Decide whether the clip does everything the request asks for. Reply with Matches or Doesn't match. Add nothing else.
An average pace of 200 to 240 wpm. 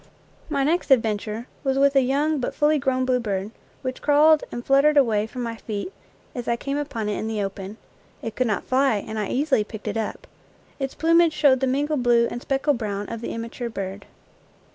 Matches